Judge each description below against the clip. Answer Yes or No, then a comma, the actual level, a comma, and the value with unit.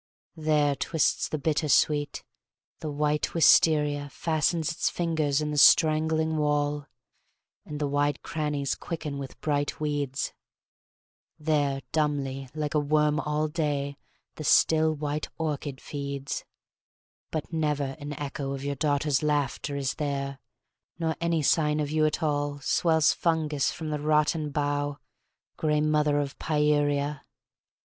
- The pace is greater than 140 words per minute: No, slow, 135 wpm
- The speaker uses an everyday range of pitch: No, narrow, 1.3 semitones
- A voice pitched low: No, medium, 150 Hz